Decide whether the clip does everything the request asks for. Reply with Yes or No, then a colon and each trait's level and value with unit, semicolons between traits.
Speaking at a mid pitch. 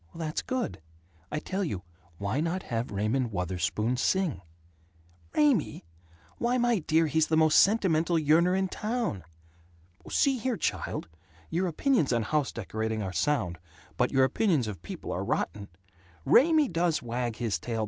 Yes: medium, 155 Hz